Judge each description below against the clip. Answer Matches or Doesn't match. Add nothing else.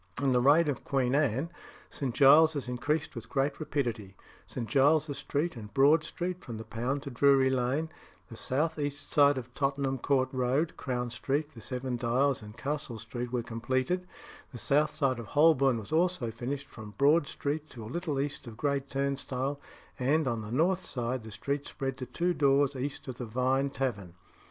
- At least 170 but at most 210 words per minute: Matches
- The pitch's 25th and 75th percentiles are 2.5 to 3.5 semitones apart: Matches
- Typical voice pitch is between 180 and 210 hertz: Doesn't match